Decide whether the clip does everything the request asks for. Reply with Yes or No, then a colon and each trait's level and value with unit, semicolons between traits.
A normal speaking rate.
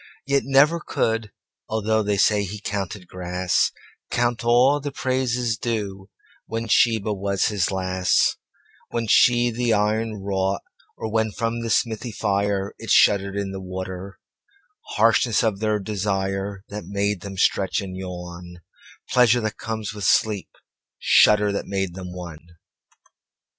No: slow, 115 wpm